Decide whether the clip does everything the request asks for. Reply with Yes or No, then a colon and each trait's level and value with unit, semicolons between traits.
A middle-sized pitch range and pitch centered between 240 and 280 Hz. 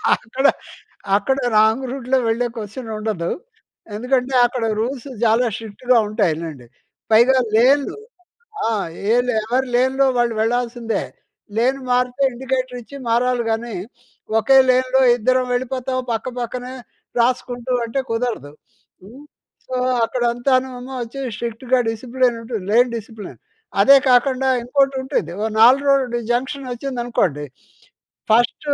No: narrow, 2.3 semitones; high, 245 Hz